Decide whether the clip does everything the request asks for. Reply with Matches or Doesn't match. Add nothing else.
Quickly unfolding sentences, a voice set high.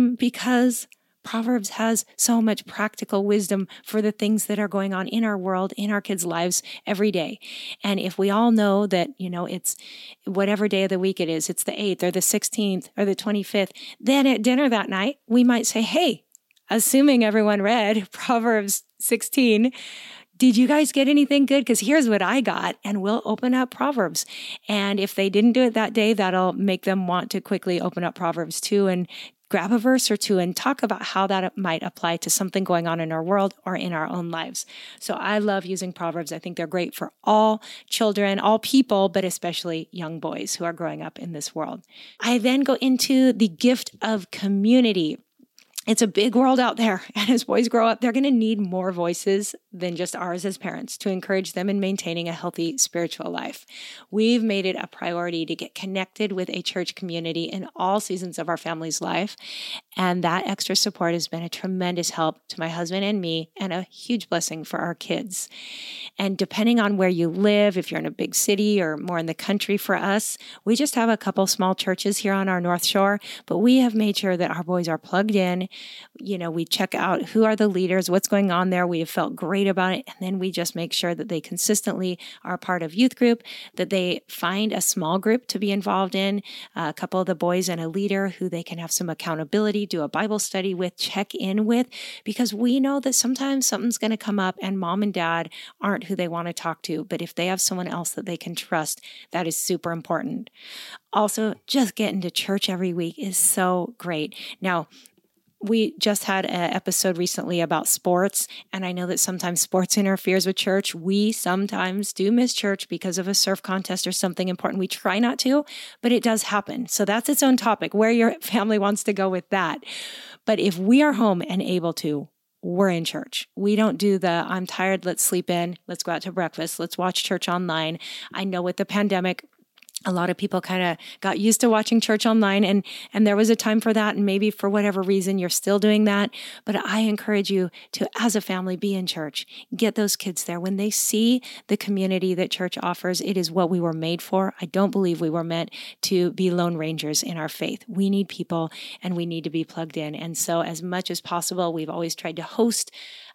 Matches